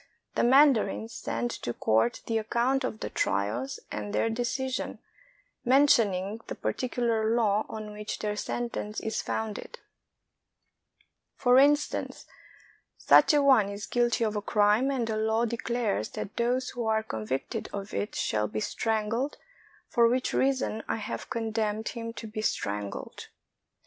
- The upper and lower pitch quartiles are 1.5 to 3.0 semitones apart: Yes, narrow, 2.6 semitones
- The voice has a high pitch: Yes, high, 220 Hz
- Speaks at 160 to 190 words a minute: No, average, 150 wpm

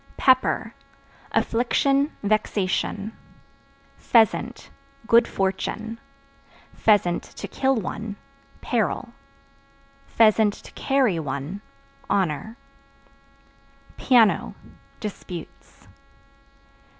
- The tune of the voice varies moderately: Yes, average, 3.4 semitones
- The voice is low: No, high, 215 Hz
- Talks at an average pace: No, slow, 55 wpm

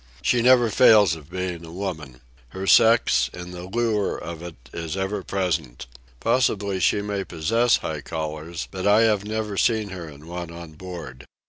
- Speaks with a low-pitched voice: Yes, very low, 95 Hz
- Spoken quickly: No, average, 170 wpm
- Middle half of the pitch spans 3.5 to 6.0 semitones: Yes, average, 4.1 semitones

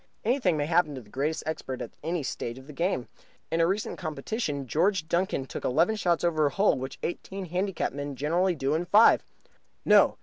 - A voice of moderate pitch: Yes, medium, 160 Hz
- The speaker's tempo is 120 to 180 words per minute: No, average, 200 wpm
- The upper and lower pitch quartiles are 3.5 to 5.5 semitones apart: Yes, average, 4.4 semitones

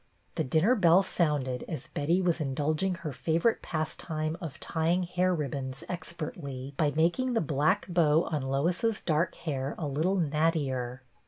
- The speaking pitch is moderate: Yes, medium, 160 Hz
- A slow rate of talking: No, average, 150 wpm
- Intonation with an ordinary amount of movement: Yes, average, 3.5 semitones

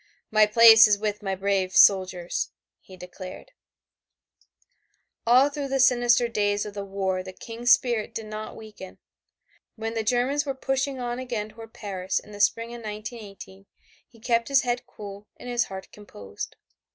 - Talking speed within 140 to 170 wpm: Yes, average, 165 wpm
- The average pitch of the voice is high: Yes, high, 215 Hz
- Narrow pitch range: No, average, 3.4 semitones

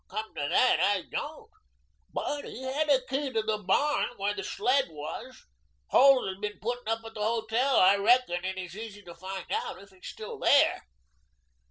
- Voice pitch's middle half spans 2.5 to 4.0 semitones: No, average, 5.3 semitones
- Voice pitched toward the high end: Yes, high, 220 Hz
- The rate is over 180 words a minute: Yes, average, 190 wpm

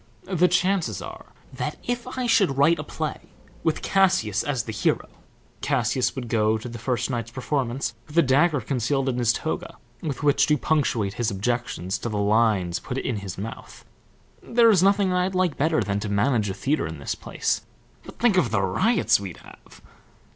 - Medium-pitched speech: No, low, 125 Hz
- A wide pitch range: Yes, wide, 7.7 semitones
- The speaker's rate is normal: Yes, average, 190 wpm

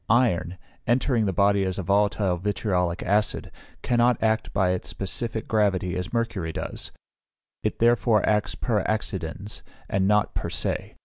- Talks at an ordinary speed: Yes, average, 145 wpm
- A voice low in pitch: Yes, low, 105 Hz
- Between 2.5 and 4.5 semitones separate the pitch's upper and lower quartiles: Yes, average, 3.1 semitones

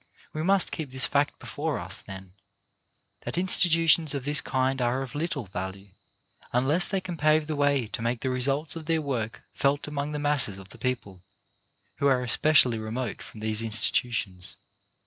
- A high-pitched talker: No, low, 135 Hz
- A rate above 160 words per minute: Yes, average, 175 wpm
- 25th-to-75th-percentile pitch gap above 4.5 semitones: Yes, average, 5.0 semitones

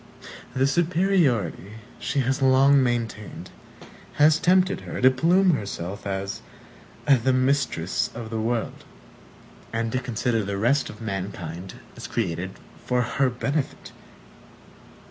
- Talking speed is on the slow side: Yes, slow, 120 wpm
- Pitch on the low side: Yes, low, 120 Hz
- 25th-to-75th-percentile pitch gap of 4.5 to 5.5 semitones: Yes, average, 5.1 semitones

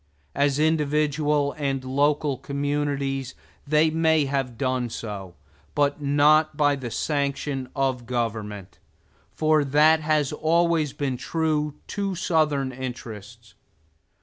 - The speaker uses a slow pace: Yes, slow, 110 wpm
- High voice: No, medium, 145 Hz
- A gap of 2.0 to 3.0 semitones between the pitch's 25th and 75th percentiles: Yes, average, 2.7 semitones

